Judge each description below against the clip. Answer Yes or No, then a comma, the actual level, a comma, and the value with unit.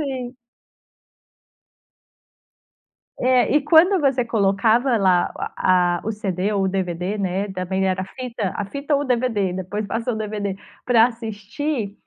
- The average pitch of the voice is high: Yes, high, 215 Hz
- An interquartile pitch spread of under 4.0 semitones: No, average, 4.6 semitones